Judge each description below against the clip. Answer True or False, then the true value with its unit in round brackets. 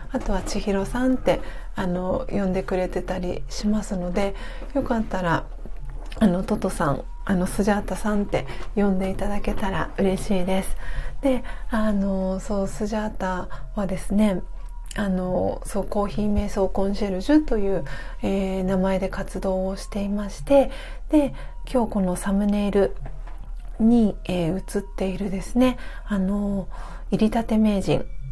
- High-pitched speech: True (200 Hz)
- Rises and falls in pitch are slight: True (2.1 semitones)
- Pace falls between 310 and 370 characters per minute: False (285 characters per minute)